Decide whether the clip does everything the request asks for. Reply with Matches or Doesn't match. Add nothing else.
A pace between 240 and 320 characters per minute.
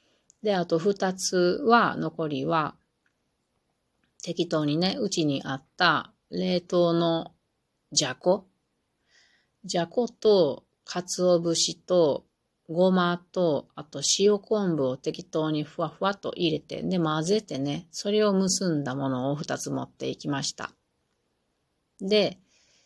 Doesn't match